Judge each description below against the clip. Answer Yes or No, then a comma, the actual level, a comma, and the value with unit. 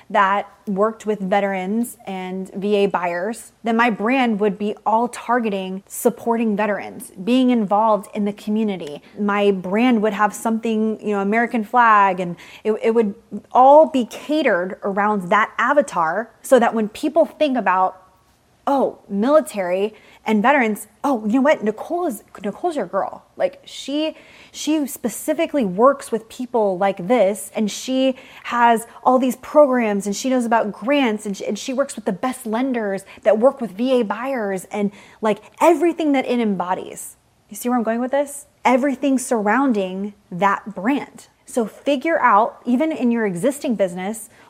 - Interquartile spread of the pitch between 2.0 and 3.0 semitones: No, average, 4.2 semitones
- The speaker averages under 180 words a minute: Yes, average, 160 wpm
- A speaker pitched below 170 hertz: No, high, 225 Hz